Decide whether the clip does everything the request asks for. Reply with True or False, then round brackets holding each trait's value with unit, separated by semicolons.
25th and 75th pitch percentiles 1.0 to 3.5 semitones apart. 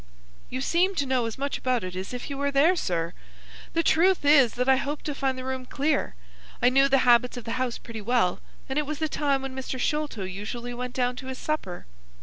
True (2.8 semitones)